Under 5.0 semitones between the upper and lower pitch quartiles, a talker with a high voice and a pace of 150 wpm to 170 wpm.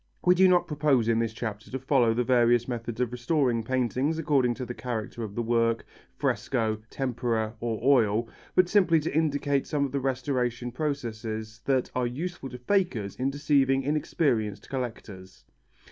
No: average, 3.5 semitones; low, 125 Hz; average, 165 wpm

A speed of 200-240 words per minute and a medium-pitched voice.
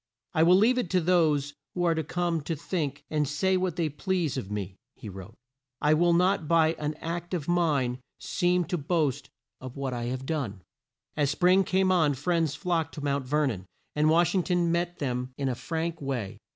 Yes: fast, 205 wpm; medium, 155 Hz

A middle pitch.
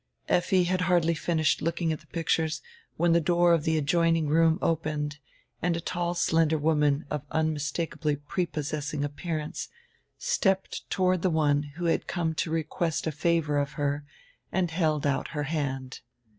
Yes: medium, 160 Hz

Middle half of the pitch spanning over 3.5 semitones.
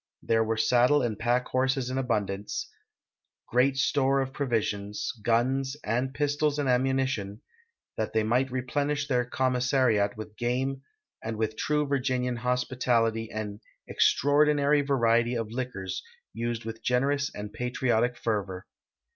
No: average, 3.0 semitones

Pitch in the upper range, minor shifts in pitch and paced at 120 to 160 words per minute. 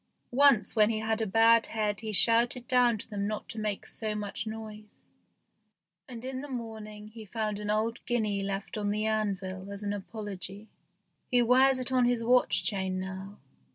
No: high, 215 Hz; narrow, 2.2 semitones; average, 185 wpm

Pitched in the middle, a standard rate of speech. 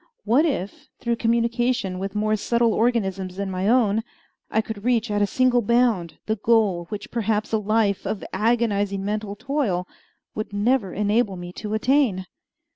No: high, 215 Hz; average, 160 wpm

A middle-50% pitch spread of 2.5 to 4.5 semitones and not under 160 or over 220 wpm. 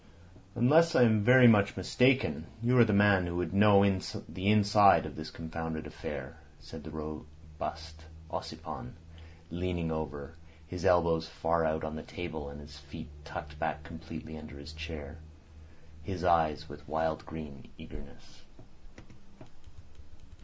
No: average, 3.5 semitones; average, 140 wpm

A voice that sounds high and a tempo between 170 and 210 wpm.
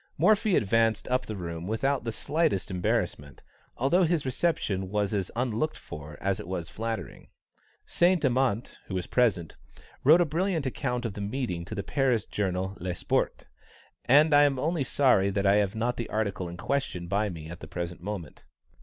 No: low, 110 Hz; average, 180 wpm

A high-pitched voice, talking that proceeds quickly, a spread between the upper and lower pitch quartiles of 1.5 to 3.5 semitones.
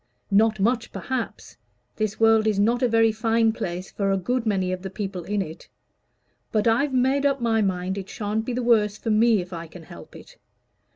Yes: high, 215 Hz; fast, 210 wpm; average, 3.2 semitones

